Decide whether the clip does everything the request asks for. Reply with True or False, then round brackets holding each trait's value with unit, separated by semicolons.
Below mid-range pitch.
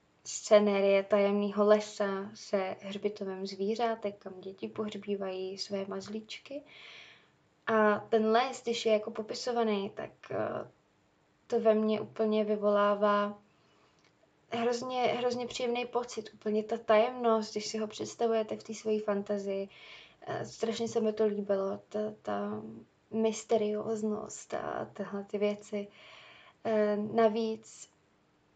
False (215 Hz)